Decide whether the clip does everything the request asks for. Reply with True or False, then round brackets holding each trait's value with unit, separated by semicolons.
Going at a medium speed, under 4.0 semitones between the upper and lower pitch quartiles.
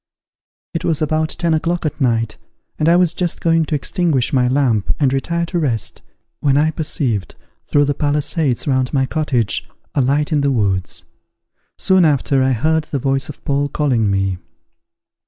True (175 wpm; 3.6 semitones)